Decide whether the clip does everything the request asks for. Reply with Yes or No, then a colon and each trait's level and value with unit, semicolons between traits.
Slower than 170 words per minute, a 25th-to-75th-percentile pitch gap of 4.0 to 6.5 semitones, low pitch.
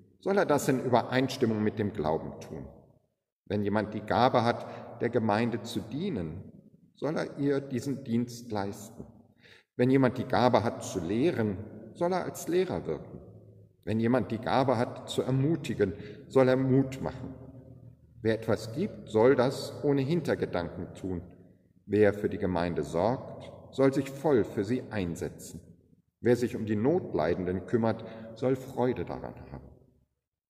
Yes: average, 150 wpm; average, 4.3 semitones; low, 115 Hz